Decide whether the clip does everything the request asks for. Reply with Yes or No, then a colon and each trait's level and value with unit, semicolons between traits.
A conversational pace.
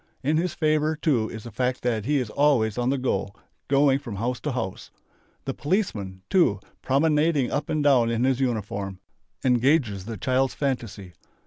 Yes: average, 175 wpm